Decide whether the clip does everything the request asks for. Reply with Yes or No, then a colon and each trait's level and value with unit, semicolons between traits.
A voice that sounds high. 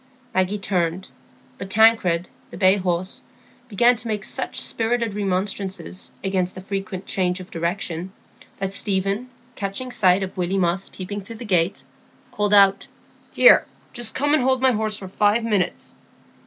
Yes: high, 195 Hz